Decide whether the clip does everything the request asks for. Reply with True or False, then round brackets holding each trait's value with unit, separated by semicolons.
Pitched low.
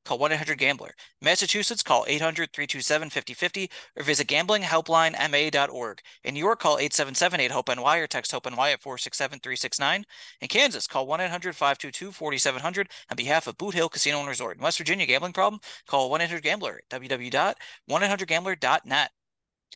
False (155 Hz)